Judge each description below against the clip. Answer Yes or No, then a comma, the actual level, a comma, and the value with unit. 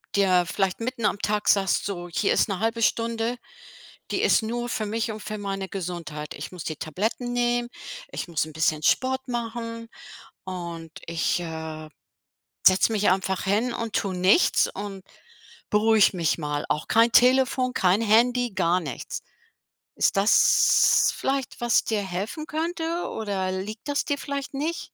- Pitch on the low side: No, high, 210 Hz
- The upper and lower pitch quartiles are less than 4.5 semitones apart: No, average, 4.8 semitones